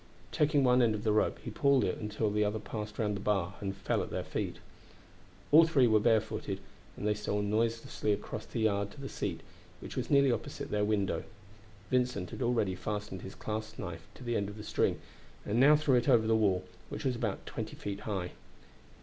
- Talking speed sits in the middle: No, fast, 215 wpm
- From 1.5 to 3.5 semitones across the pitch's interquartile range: Yes, average, 2.9 semitones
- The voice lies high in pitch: No, low, 110 Hz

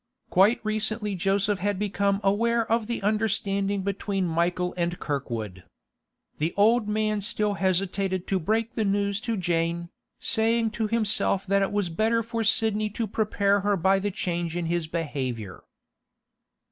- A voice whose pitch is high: Yes, high, 200 Hz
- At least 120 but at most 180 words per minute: Yes, average, 150 wpm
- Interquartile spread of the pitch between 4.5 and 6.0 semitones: No, average, 3.3 semitones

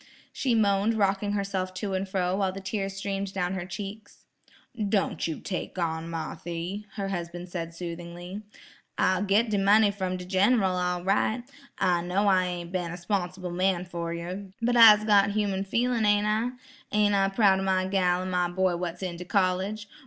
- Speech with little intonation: Yes, narrow, 2.3 semitones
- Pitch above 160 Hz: Yes, high, 190 Hz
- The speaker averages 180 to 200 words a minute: Yes, average, 190 wpm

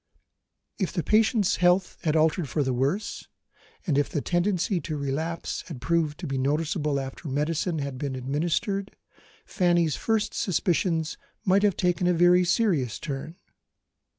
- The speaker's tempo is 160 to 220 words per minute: No, average, 150 wpm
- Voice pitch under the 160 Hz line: No, medium, 165 Hz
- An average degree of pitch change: Yes, average, 3.9 semitones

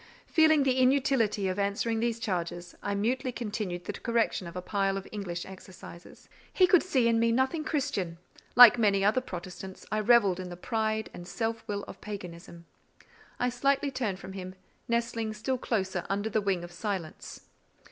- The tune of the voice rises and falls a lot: No, average, 4.2 semitones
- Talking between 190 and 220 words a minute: No, average, 175 wpm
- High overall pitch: Yes, high, 210 Hz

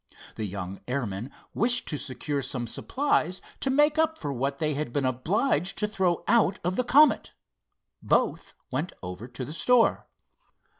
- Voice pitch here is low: No, medium, 150 Hz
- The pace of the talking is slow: No, average, 160 wpm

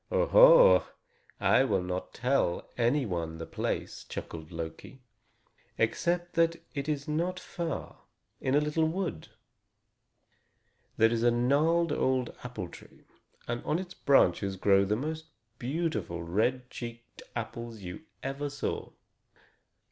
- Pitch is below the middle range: Yes, low, 125 Hz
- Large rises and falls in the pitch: Yes, wide, 7.2 semitones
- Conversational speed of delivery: No, slow, 125 wpm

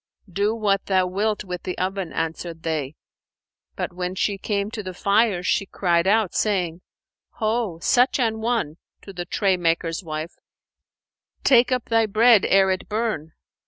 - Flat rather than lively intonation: No, average, 3.7 semitones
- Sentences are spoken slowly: No, average, 160 wpm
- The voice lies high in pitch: Yes, high, 195 Hz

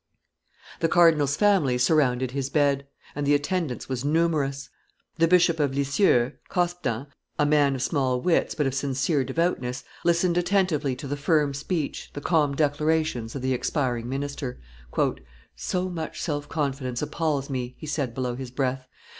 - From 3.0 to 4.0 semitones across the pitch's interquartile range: Yes, average, 3.6 semitones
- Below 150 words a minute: No, average, 155 wpm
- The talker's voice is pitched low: No, medium, 145 Hz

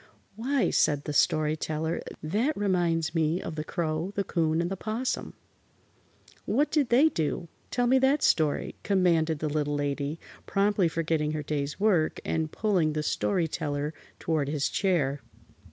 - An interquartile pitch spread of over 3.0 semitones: Yes, average, 4.7 semitones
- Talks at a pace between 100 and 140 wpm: No, average, 155 wpm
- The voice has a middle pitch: Yes, medium, 165 Hz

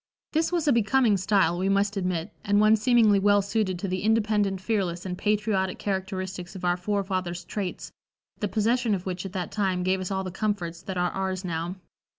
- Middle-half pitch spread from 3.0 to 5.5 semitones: No, narrow, 2.4 semitones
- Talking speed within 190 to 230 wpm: Yes, average, 195 wpm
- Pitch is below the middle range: No, high, 195 Hz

